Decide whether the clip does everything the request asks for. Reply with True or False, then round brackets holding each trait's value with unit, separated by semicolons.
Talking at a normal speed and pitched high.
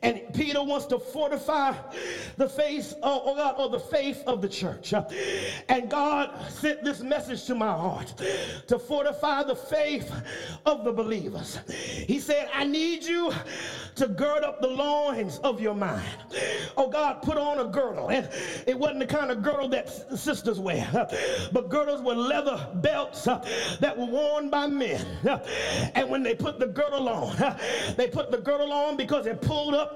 True (170 wpm; 280 Hz)